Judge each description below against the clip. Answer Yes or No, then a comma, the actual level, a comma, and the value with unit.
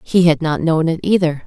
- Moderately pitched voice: Yes, medium, 165 Hz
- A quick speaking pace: Yes, fast, 245 wpm